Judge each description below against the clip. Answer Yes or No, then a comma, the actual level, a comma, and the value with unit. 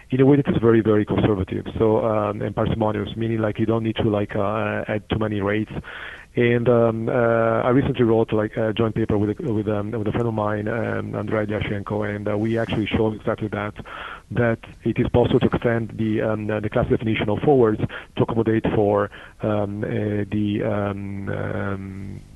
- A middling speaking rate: Yes, average, 195 wpm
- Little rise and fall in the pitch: Yes, narrow, 1.6 semitones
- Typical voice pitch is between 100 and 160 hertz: Yes, low, 110 Hz